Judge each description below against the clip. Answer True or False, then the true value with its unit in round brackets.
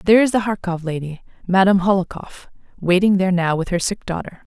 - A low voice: False (185 Hz)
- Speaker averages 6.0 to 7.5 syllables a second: True (6.1 syllables/s)